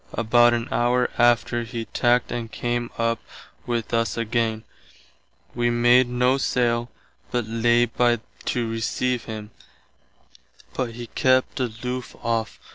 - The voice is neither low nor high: No, low, 120 Hz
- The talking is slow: Yes, slow, 125 wpm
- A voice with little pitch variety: Yes, narrow, 1.0 semitones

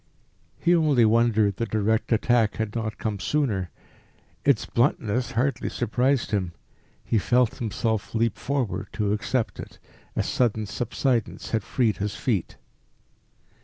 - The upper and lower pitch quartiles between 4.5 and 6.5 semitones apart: No, average, 2.8 semitones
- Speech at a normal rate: No, slow, 130 wpm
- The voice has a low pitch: Yes, low, 115 Hz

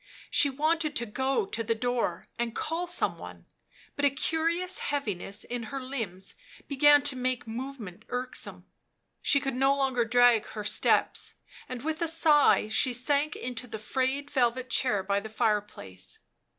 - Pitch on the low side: No, very high, 255 Hz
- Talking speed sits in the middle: Yes, average, 160 wpm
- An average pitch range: Yes, average, 4.2 semitones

